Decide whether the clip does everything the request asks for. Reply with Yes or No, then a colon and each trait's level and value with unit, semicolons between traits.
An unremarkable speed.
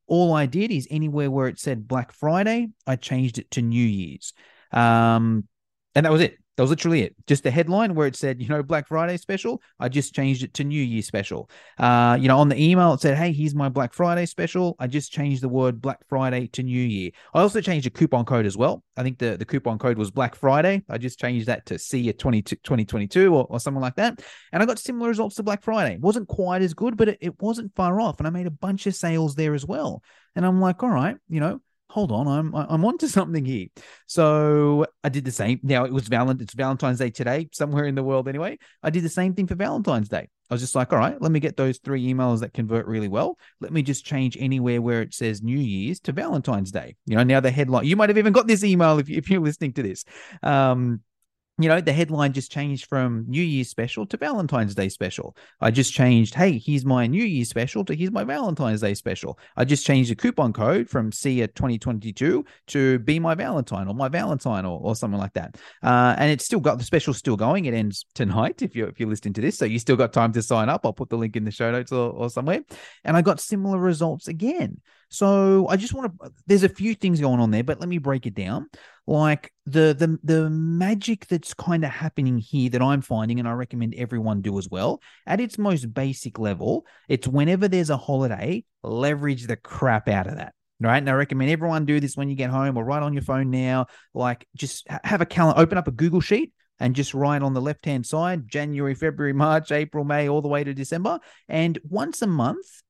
No: fast, 240 wpm